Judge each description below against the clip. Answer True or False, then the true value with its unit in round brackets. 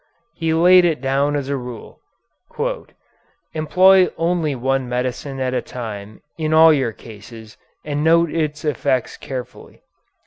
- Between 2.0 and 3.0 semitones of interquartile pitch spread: False (4.4 semitones)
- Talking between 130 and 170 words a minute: True (135 wpm)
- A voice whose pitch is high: False (140 Hz)